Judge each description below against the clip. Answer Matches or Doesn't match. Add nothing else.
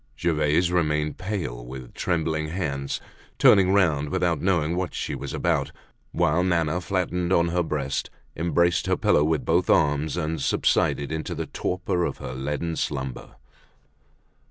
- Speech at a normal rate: Matches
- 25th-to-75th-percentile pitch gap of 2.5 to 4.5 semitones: Matches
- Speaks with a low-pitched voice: Matches